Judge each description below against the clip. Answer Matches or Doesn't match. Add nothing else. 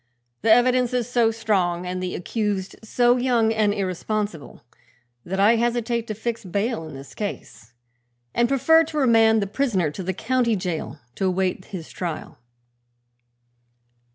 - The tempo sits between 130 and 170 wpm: Matches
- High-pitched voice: Matches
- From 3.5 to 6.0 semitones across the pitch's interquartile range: Matches